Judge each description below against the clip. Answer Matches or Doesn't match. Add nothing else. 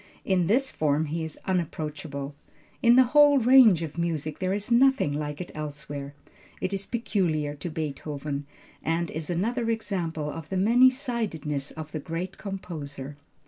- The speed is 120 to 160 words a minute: Matches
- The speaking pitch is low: Doesn't match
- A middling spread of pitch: Doesn't match